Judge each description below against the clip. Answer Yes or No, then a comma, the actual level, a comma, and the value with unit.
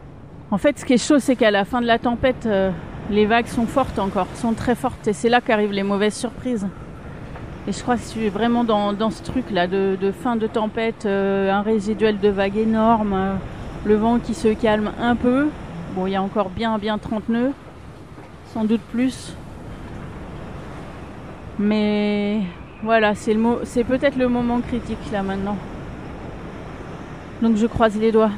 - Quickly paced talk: No, average, 180 wpm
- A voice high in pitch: Yes, high, 220 Hz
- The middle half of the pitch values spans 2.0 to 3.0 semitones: Yes, average, 2.7 semitones